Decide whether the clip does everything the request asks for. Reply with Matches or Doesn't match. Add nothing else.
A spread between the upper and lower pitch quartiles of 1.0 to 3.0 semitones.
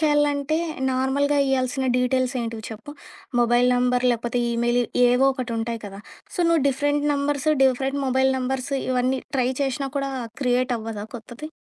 Matches